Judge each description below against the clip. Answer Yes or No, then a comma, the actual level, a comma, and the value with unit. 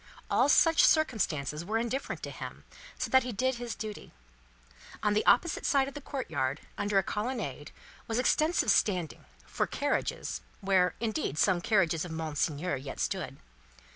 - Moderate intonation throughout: No, wide, 7.7 semitones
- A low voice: No, high, 210 Hz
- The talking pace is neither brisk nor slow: Yes, average, 155 wpm